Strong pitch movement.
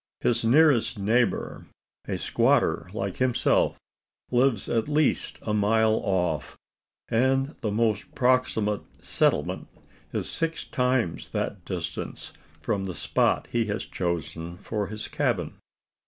No: average, 4.2 semitones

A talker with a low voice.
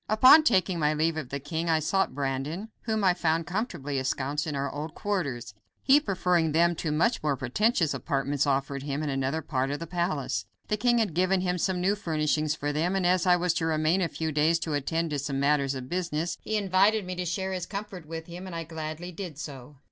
No: medium, 165 Hz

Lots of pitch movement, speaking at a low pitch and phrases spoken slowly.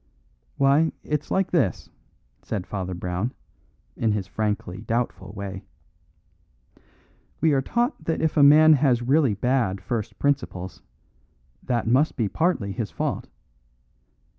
Yes: wide, 6.9 semitones; low, 120 Hz; slow, 125 wpm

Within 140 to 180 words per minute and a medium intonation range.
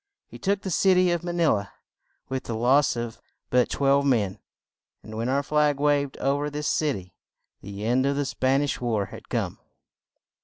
No: average, 200 wpm; average, 3.8 semitones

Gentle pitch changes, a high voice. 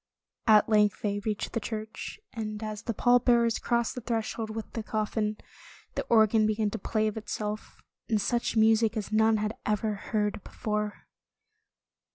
Yes: narrow, 1.1 semitones; high, 215 Hz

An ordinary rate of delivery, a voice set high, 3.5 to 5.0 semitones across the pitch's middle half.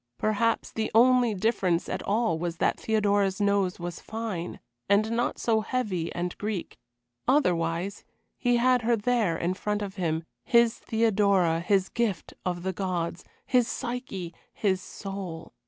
Yes: average, 145 wpm; high, 200 Hz; average, 4.2 semitones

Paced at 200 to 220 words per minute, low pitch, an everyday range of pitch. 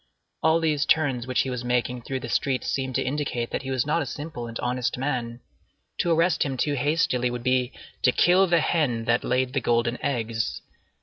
Yes: fast, 205 wpm; low, 130 Hz; average, 3.3 semitones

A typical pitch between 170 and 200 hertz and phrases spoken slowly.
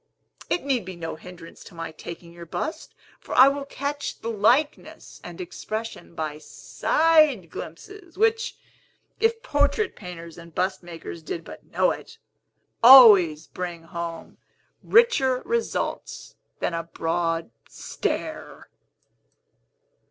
Yes: high, 190 Hz; slow, 120 wpm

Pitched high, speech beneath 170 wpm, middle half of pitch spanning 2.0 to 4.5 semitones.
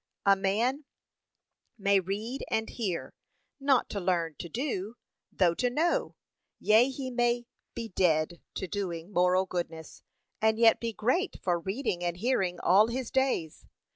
No: high, 205 Hz; average, 145 wpm; average, 5.3 semitones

